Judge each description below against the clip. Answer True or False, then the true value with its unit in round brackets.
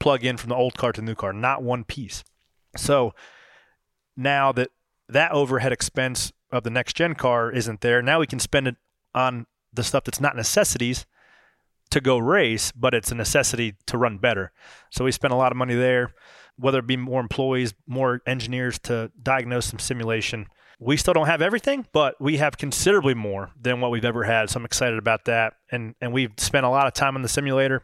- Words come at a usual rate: False (210 wpm)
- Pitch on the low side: True (125 Hz)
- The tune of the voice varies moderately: False (2.2 semitones)